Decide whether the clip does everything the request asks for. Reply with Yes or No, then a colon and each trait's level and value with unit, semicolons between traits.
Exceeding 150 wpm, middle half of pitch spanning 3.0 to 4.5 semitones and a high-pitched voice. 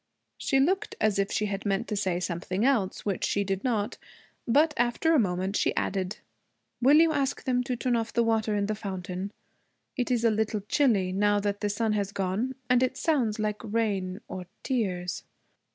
Yes: average, 195 wpm; average, 3.9 semitones; high, 210 Hz